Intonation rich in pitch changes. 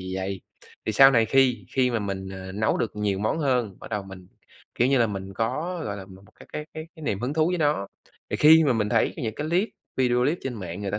Yes: wide, 5.7 semitones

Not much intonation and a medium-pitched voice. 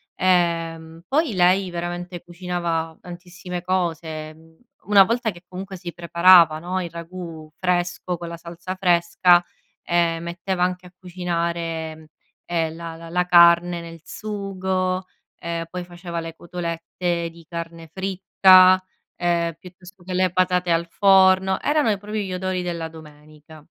Yes: narrow, 1.6 semitones; medium, 175 Hz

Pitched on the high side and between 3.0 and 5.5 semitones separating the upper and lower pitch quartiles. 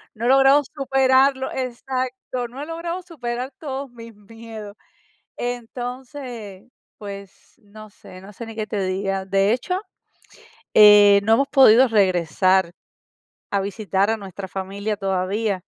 Yes: high, 225 Hz; average, 4.6 semitones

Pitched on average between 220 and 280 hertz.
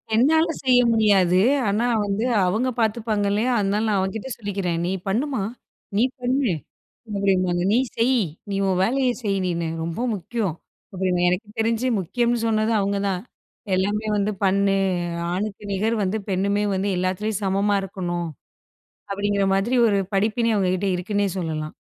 No: high, 200 Hz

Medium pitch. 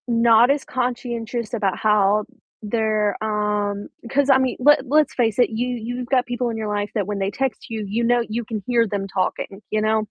No: high, 225 Hz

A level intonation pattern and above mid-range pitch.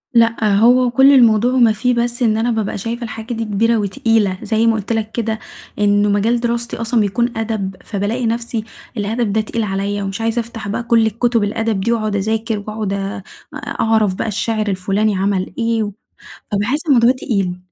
Yes: narrow, 2.3 semitones; high, 220 Hz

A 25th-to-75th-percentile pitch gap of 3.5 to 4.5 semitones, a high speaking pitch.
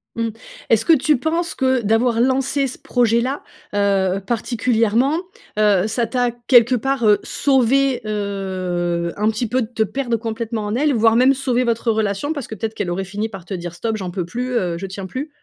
Yes: average, 4.0 semitones; high, 225 Hz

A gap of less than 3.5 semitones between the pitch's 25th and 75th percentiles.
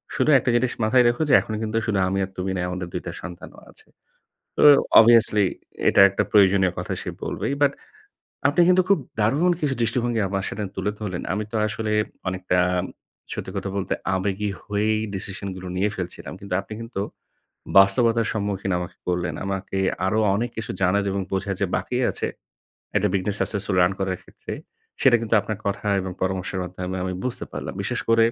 Yes: average, 3.1 semitones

